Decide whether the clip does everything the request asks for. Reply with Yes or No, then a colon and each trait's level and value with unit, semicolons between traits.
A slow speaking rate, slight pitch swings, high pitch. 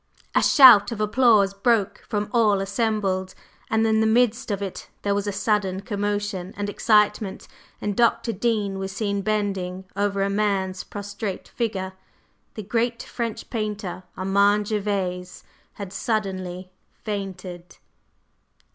Yes: slow, 130 wpm; narrow, 1.9 semitones; high, 205 Hz